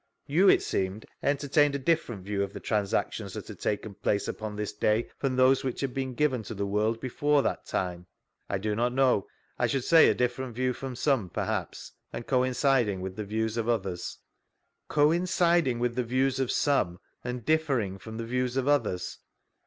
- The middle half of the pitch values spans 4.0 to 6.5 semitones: Yes, average, 4.3 semitones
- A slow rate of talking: No, average, 190 wpm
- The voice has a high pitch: No, low, 125 Hz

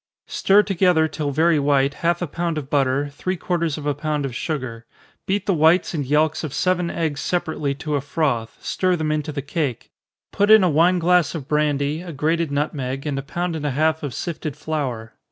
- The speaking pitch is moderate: Yes, medium, 155 Hz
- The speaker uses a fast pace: Yes, fast, 210 wpm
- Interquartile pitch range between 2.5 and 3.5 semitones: Yes, average, 3.1 semitones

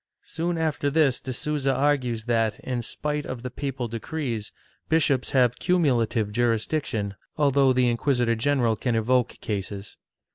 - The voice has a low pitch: Yes, low, 125 Hz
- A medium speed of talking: Yes, average, 145 wpm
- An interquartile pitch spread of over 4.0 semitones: No, average, 3.7 semitones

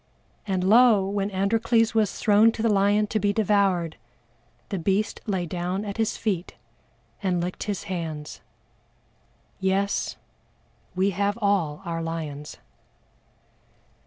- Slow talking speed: Yes, slow, 125 wpm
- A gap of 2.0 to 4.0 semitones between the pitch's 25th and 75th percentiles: Yes, average, 2.8 semitones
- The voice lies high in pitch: Yes, high, 195 Hz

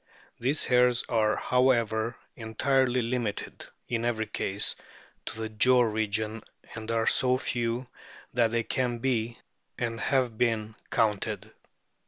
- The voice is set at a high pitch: No, low, 115 Hz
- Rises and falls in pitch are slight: Yes, narrow, 2.1 semitones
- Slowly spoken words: Yes, slow, 125 wpm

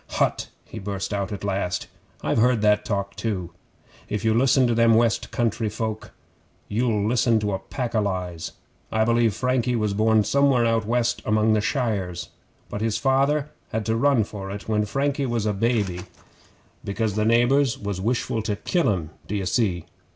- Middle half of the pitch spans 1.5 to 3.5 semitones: Yes, average, 2.8 semitones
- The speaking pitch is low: Yes, low, 110 Hz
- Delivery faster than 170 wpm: Yes, average, 180 wpm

